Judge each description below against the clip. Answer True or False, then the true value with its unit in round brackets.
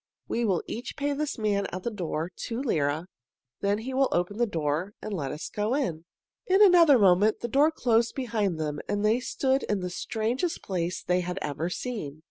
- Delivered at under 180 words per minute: False (200 wpm)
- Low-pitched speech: False (210 Hz)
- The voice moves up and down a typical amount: False (6.0 semitones)